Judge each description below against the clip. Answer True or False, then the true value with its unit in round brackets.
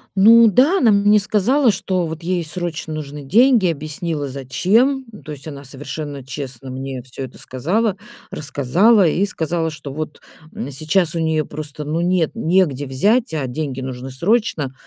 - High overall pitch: False (160 Hz)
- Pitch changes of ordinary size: False (6.0 semitones)